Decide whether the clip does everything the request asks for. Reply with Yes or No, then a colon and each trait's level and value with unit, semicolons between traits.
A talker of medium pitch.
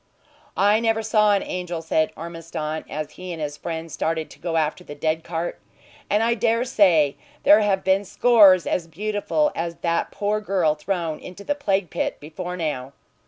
Yes: medium, 180 Hz